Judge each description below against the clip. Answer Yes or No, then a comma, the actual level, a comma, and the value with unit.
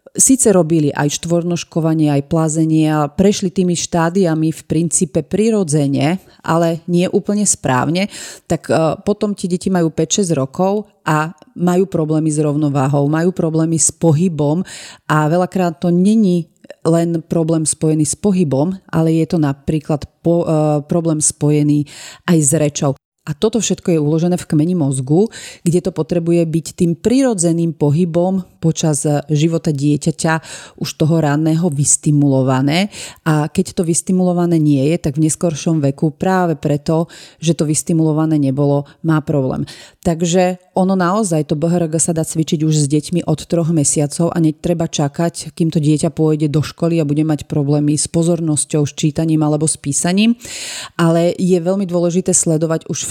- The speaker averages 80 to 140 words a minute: No, average, 150 wpm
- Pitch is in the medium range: Yes, medium, 165 Hz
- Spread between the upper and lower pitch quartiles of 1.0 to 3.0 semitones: Yes, narrow, 2.5 semitones